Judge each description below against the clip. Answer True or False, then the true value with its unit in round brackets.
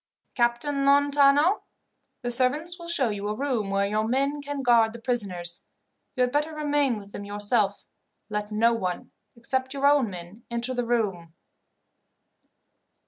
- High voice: True (240 Hz)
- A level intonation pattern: False (5.1 semitones)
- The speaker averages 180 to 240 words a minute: False (150 wpm)